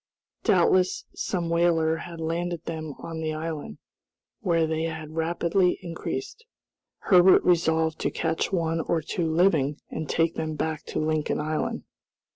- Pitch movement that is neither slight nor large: No, narrow, 1.5 semitones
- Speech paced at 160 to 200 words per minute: No, average, 140 wpm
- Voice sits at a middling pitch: Yes, medium, 165 Hz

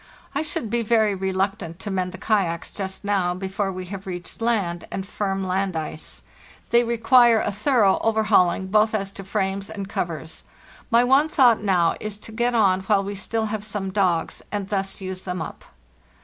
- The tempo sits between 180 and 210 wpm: Yes, average, 185 wpm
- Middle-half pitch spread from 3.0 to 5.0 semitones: No, narrow, 2.6 semitones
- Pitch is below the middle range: No, high, 195 Hz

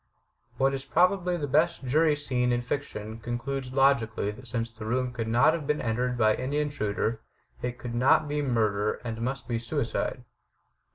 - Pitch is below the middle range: Yes, low, 125 Hz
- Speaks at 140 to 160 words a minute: No, average, 175 wpm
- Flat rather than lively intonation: No, average, 3.6 semitones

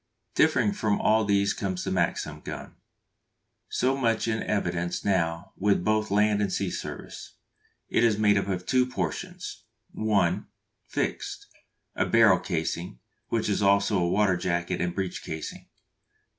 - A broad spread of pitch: No, average, 3.3 semitones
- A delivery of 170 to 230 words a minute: No, average, 150 wpm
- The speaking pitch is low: Yes, low, 100 Hz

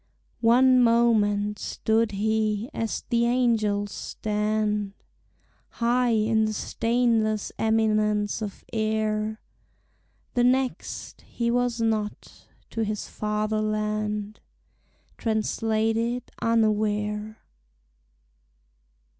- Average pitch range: No, narrow, 1.5 semitones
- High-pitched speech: Yes, high, 220 Hz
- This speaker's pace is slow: Yes, slow, 80 wpm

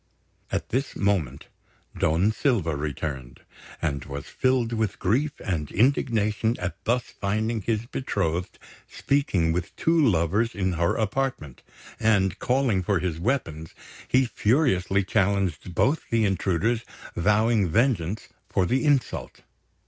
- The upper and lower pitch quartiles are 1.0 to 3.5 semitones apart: No, wide, 5.6 semitones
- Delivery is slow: Yes, slow, 125 wpm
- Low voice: Yes, low, 100 Hz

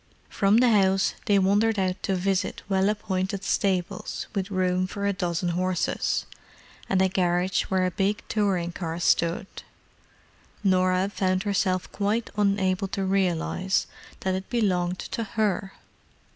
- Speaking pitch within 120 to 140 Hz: No, high, 190 Hz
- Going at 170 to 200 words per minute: No, slow, 135 wpm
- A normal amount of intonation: No, narrow, 1.5 semitones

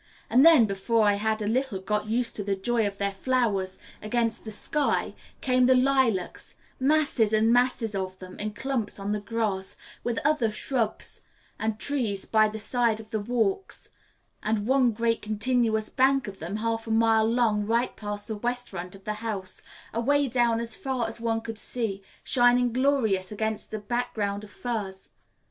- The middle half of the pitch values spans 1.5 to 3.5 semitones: Yes, average, 2.9 semitones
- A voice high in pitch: Yes, high, 225 Hz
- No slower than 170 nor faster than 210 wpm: Yes, average, 175 wpm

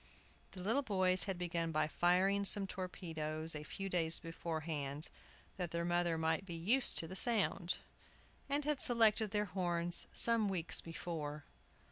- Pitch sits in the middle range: Yes, medium, 175 Hz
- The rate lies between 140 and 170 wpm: Yes, average, 150 wpm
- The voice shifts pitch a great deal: No, average, 3.2 semitones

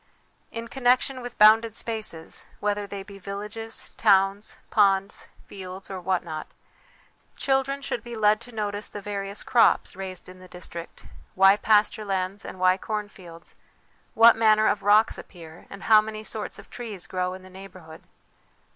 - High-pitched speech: Yes, high, 205 Hz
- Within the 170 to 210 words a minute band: No, average, 155 wpm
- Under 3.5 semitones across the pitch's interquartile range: Yes, average, 2.7 semitones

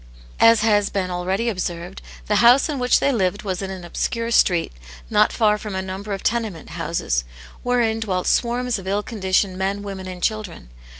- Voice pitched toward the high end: Yes, high, 200 Hz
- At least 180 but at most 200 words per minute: Yes, average, 185 wpm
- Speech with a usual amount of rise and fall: Yes, average, 3.5 semitones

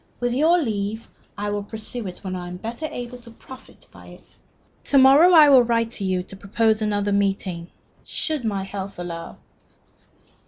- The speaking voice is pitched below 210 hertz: No, high, 215 Hz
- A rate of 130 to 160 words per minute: No, average, 180 wpm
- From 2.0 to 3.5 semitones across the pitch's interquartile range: No, average, 4.1 semitones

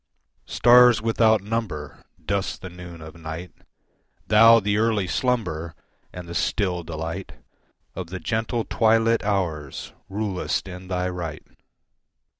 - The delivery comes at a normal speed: No, slow, 120 wpm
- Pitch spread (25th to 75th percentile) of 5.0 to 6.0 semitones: No, average, 4.5 semitones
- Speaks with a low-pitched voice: Yes, very low, 95 Hz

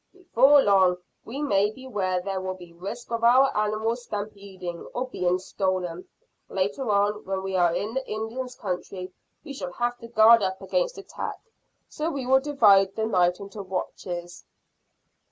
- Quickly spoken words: No, average, 160 wpm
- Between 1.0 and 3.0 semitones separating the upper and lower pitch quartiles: No, average, 4.6 semitones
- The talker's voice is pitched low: No, high, 210 Hz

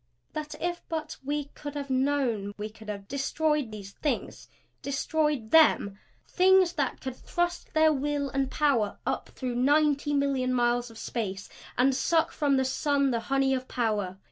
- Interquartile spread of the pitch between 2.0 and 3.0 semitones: No, average, 3.8 semitones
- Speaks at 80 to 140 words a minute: No, average, 165 wpm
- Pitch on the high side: Yes, very high, 275 Hz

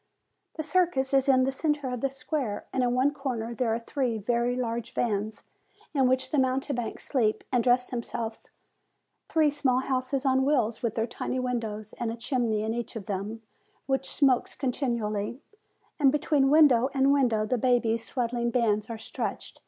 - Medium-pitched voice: No, very high, 250 Hz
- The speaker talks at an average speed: Yes, average, 175 wpm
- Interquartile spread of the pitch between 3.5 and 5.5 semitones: No, average, 2.9 semitones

